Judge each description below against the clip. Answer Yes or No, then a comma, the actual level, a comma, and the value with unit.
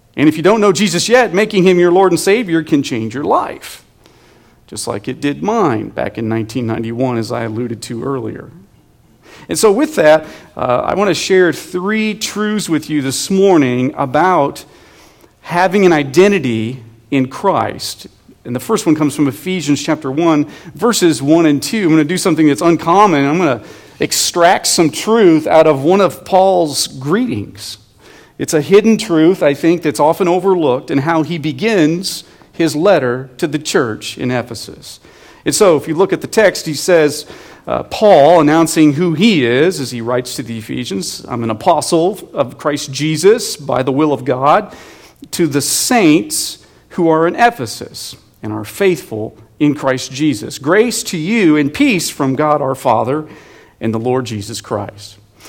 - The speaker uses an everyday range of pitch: No, wide, 6.0 semitones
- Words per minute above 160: Yes, average, 175 wpm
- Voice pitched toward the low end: No, medium, 155 Hz